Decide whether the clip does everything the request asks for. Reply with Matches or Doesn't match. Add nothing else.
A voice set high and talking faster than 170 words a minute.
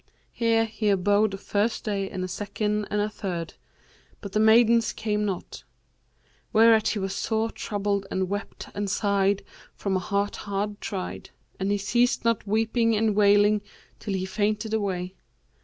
Doesn't match